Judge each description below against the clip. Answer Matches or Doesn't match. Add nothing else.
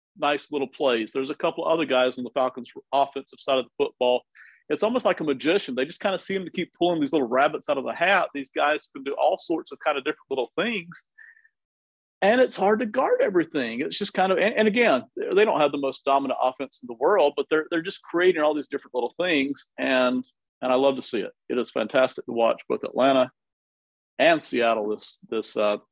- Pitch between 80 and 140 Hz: Doesn't match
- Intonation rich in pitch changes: Matches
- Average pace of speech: Doesn't match